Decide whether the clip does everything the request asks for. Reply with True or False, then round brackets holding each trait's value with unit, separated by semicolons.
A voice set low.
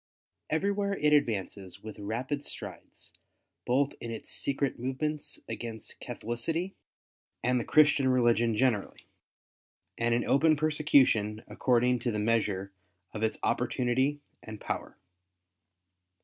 True (125 Hz)